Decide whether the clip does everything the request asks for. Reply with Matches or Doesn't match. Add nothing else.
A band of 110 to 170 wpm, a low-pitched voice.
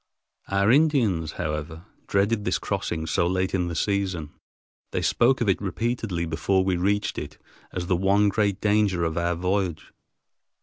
Matches